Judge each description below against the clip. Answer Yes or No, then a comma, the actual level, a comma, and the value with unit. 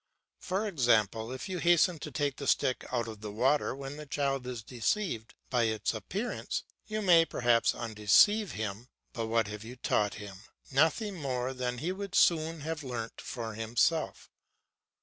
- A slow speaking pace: No, average, 170 wpm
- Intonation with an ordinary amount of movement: No, wide, 6.3 semitones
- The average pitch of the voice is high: No, low, 130 Hz